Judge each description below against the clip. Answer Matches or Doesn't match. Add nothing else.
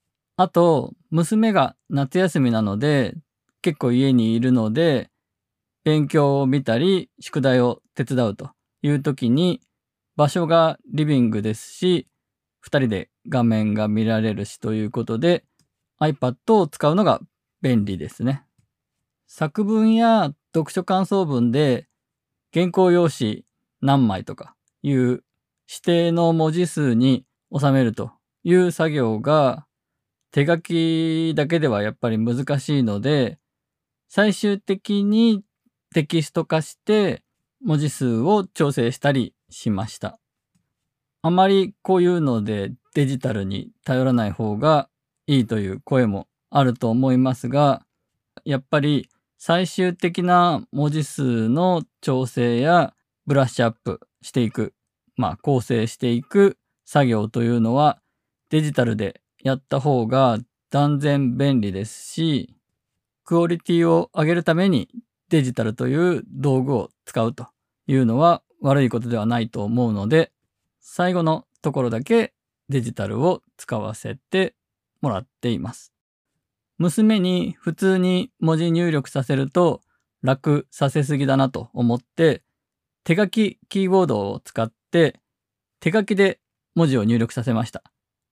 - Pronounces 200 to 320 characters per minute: Matches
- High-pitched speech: Doesn't match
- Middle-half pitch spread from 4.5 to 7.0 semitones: Matches